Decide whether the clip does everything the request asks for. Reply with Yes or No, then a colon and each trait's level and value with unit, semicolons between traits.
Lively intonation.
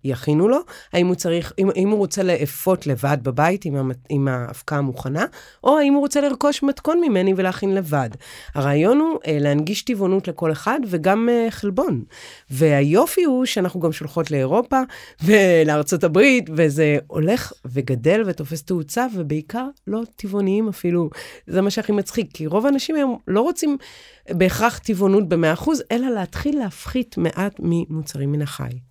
Yes: wide, 7.2 semitones